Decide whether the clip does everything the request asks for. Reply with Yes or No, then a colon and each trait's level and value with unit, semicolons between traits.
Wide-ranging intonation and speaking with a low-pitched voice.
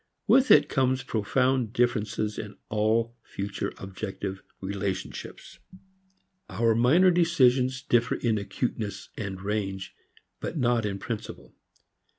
No: average, 4.0 semitones; low, 110 Hz